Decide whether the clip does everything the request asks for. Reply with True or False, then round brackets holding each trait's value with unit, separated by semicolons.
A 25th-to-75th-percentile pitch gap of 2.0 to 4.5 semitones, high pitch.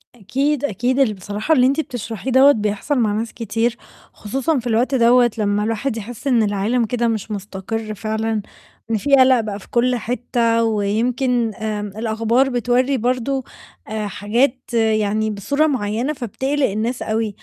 True (2.9 semitones; 230 Hz)